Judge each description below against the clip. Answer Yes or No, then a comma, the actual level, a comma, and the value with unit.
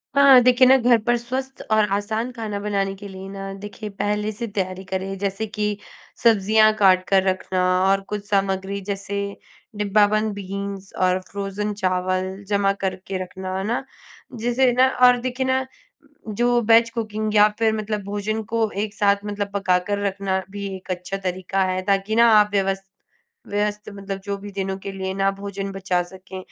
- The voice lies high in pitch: Yes, high, 200 Hz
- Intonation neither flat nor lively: No, narrow, 2.0 semitones